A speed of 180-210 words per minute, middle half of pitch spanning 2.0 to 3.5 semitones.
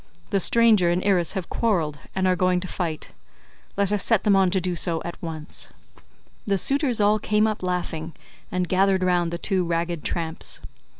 Yes: average, 185 wpm; average, 2.7 semitones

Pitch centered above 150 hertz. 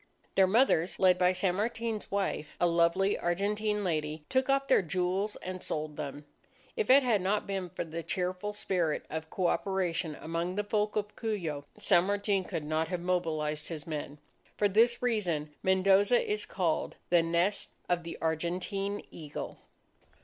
Yes: medium, 185 Hz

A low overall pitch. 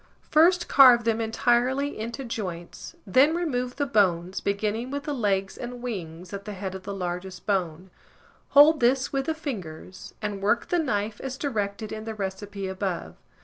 No: high, 215 Hz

